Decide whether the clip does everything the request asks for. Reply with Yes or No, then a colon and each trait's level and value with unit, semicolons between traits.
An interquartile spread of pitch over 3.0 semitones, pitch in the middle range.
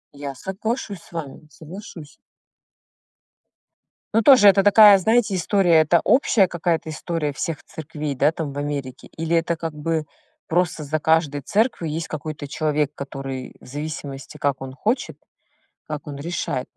Yes: average, 3.7 semitones; medium, 160 Hz